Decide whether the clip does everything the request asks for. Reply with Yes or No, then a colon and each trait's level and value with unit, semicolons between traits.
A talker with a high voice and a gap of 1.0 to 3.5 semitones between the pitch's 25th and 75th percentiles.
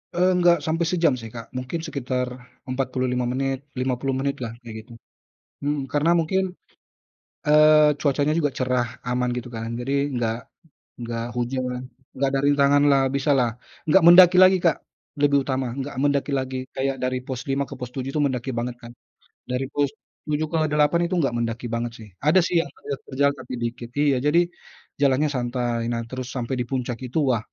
No: low, 135 Hz; average, 2.9 semitones